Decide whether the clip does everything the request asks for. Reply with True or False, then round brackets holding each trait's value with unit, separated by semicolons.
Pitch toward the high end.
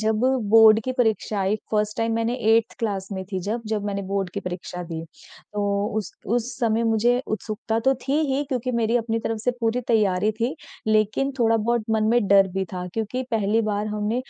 True (220 Hz)